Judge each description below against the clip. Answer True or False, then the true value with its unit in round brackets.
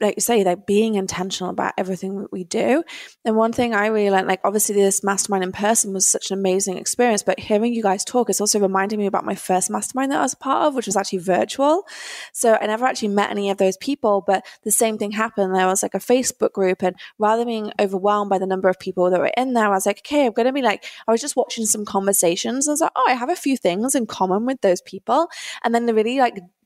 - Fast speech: True (265 wpm)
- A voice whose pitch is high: True (210 Hz)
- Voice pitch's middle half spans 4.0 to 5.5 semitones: False (3.6 semitones)